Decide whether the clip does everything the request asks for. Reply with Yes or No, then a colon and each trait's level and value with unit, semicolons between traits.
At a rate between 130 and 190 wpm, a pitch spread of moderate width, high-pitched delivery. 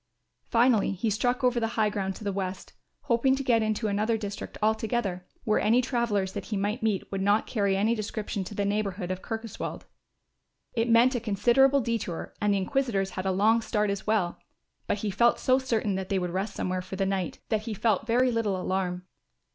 No: fast, 205 wpm; average, 3.1 semitones; high, 210 Hz